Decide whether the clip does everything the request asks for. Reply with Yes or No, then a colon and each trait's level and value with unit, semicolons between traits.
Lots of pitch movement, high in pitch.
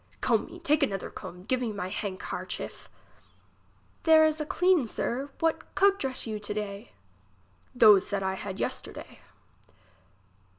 Yes: wide, 7.3 semitones; high, 225 Hz